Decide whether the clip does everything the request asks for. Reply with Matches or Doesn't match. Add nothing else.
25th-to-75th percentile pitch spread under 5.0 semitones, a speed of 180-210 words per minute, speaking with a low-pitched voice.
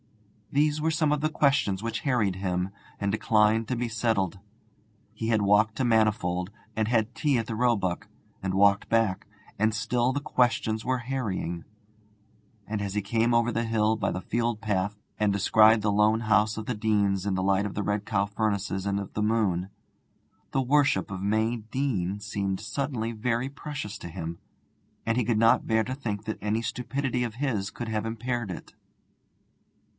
Matches